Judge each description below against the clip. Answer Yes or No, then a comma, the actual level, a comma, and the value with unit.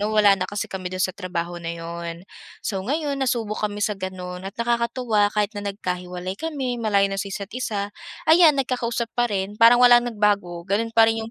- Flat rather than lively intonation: No, average, 3.9 semitones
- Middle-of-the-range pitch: No, high, 205 Hz